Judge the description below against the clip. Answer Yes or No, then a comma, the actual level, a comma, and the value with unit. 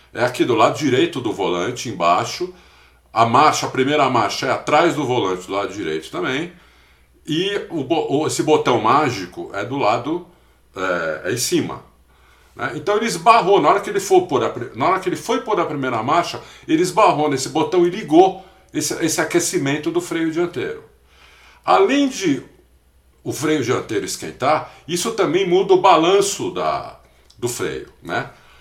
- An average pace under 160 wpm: No, average, 170 wpm